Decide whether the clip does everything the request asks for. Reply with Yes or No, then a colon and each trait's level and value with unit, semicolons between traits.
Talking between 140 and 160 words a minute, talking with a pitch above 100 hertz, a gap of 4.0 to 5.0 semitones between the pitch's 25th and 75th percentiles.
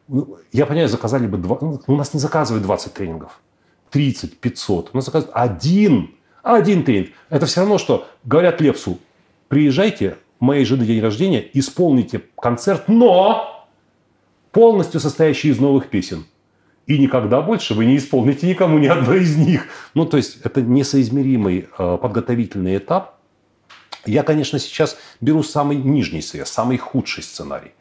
Yes: average, 145 wpm; medium, 140 Hz; average, 4.5 semitones